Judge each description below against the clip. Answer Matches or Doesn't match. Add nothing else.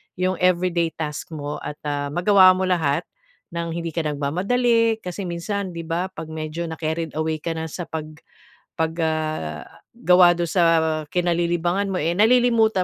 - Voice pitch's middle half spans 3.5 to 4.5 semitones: Doesn't match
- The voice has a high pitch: Doesn't match